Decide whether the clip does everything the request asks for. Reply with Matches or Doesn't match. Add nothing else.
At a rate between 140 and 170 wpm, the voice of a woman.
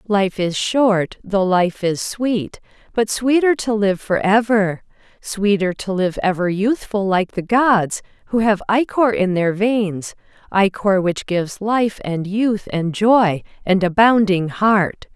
Matches